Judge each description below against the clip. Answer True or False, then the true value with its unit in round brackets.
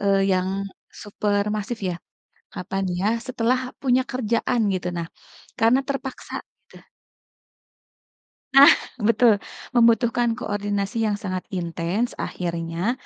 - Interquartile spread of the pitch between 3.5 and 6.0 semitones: True (4.4 semitones)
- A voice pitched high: True (210 Hz)